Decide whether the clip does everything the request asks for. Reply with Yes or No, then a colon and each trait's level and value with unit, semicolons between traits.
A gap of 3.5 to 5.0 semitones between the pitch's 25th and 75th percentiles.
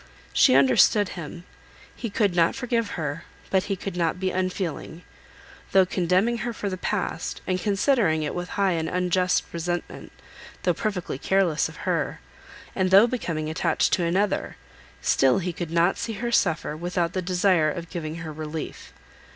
No: average, 2.9 semitones